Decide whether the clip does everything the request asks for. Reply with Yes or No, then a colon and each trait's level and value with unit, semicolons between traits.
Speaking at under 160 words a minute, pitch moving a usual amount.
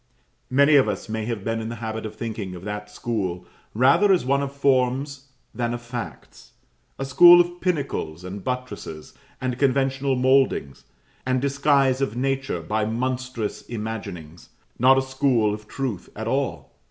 No: average, 165 wpm; average, 4.0 semitones